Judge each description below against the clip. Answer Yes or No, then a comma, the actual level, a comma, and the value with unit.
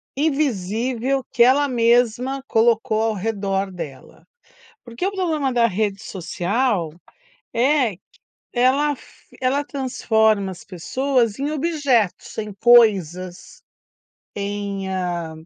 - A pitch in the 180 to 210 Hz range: No, high, 230 Hz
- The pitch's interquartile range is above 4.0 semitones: Yes, average, 5.2 semitones